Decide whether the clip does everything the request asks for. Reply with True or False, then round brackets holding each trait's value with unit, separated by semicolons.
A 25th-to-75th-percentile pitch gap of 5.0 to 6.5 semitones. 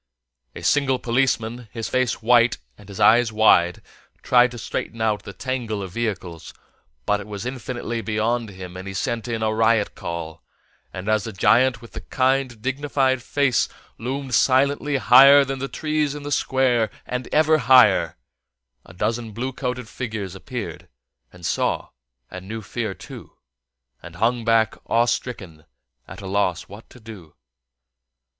False (3.7 semitones)